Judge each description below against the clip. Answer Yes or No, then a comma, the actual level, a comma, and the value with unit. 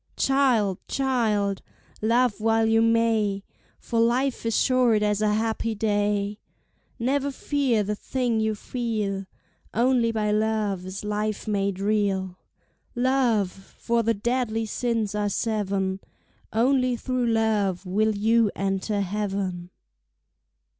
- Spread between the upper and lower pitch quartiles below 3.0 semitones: Yes, narrow, 2.5 semitones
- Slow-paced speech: Yes, slow, 120 wpm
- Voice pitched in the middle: No, high, 220 Hz